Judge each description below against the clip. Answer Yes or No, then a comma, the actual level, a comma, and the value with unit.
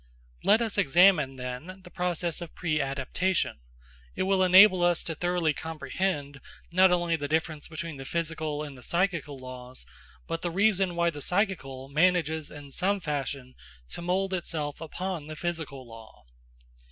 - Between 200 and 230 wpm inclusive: No, average, 155 wpm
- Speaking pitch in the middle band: Yes, medium, 165 Hz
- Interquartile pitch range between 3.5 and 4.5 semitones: Yes, average, 4.0 semitones